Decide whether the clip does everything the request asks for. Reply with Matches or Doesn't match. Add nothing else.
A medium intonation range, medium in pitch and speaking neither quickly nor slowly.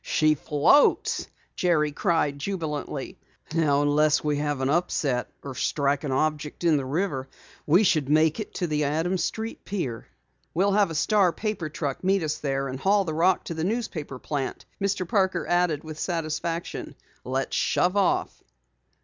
Matches